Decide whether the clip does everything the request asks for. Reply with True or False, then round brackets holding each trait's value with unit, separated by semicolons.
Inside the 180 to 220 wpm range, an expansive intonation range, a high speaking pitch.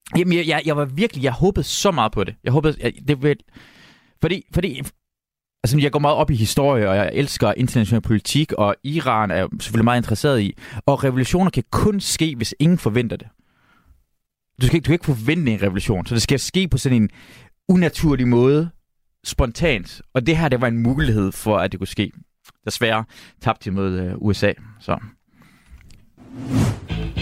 False (185 wpm; 5.7 semitones; 125 Hz)